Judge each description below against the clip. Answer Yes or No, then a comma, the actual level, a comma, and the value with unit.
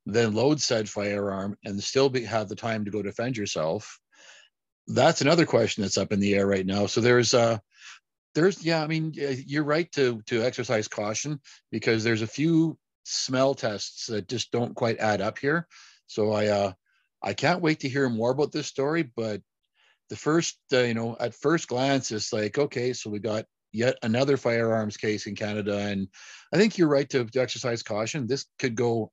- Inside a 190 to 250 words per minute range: Yes, average, 200 wpm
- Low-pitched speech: Yes, low, 120 Hz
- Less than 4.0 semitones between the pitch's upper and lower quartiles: No, average, 4.5 semitones